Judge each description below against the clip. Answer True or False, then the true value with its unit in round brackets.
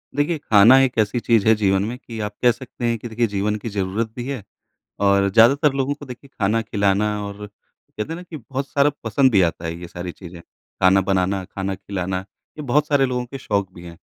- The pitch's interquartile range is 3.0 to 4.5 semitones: False (4.9 semitones)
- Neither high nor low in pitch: False (110 Hz)